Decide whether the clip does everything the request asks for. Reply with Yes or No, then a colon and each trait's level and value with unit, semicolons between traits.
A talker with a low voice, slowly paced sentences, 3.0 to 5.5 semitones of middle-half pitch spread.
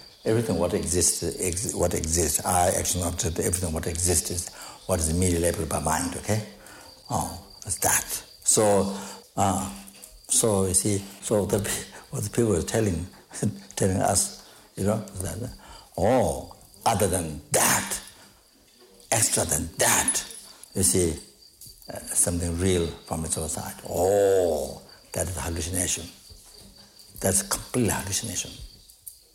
No: very low, 90 Hz; slow, 130 wpm; narrow, 2.6 semitones